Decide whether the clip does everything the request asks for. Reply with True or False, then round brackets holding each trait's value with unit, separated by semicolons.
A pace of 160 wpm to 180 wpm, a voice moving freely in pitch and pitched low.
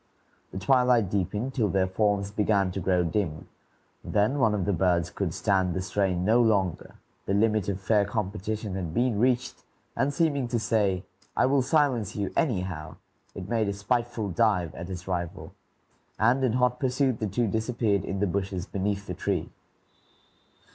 False (170 wpm; 4.0 semitones; 100 Hz)